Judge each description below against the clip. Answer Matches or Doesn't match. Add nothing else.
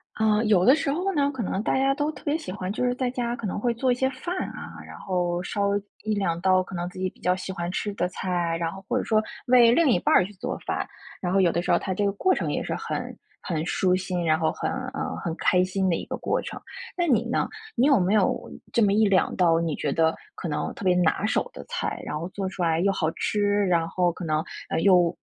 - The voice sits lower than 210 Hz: Matches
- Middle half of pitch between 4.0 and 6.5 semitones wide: Matches